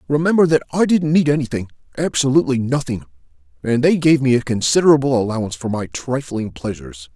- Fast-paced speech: No, average, 160 wpm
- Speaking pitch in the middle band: No, low, 130 Hz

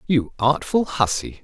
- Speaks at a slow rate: Yes, slow, 125 wpm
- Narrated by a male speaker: Yes, male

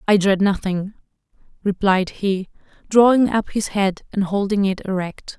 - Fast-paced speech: No, average, 145 wpm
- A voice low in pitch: No, high, 200 Hz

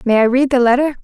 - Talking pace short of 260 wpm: No, fast, 290 wpm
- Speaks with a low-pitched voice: No, very high, 255 Hz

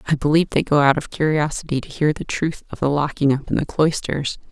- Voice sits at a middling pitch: Yes, medium, 145 Hz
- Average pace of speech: No, fast, 240 wpm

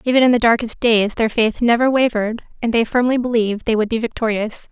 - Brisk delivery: Yes, fast, 215 wpm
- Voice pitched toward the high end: Yes, high, 230 Hz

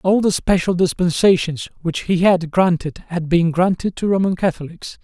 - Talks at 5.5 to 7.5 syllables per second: No, 4.9 syllables/s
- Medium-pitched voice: Yes, medium, 175 Hz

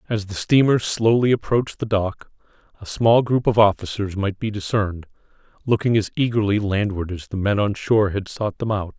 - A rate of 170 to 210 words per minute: Yes, average, 185 wpm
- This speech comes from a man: Yes, male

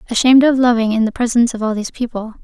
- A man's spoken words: No, female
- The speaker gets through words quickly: Yes, fast, 245 wpm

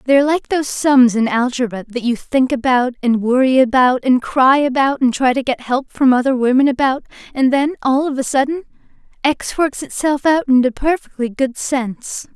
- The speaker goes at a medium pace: Yes, average, 195 wpm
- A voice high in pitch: Yes, very high, 260 Hz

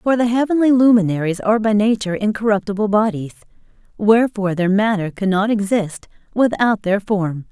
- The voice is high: Yes, high, 210 Hz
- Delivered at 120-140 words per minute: Yes, slow, 135 wpm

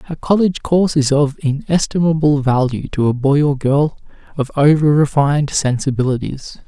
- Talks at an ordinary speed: Yes, average, 145 wpm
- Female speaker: No, male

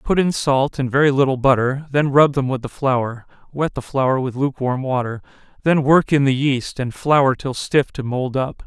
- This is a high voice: No, low, 135 Hz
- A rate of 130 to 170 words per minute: No, average, 195 wpm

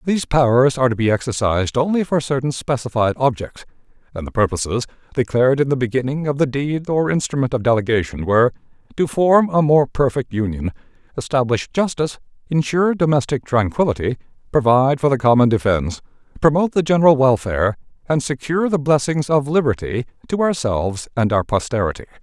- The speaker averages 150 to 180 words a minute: Yes, average, 155 wpm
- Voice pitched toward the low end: Yes, low, 130 Hz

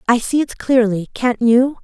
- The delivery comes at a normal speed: Yes, average, 195 wpm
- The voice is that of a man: No, female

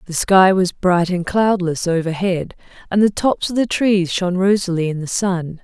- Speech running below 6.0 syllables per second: Yes, 4.7 syllables/s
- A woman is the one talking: Yes, female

